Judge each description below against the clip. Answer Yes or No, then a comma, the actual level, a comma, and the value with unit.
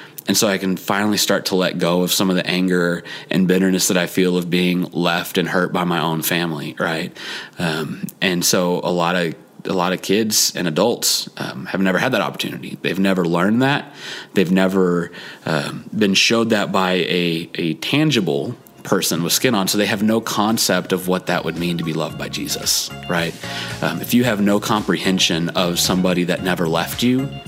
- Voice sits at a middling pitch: No, very low, 90 Hz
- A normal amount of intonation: No, narrow, 2.3 semitones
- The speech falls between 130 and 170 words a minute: No, fast, 205 wpm